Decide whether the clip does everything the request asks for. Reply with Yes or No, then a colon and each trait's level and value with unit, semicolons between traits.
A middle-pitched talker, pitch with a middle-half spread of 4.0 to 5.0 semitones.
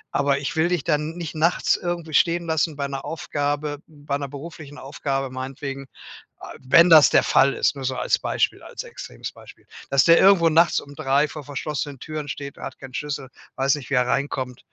No: medium, 145 Hz; narrow, 2.6 semitones